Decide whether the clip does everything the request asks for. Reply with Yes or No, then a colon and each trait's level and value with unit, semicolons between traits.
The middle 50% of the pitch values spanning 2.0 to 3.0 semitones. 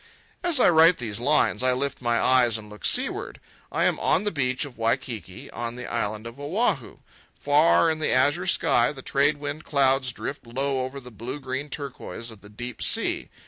No: average, 3.5 semitones